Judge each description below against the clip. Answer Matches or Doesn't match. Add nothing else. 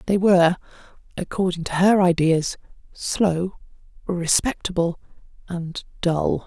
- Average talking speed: Doesn't match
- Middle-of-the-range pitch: Matches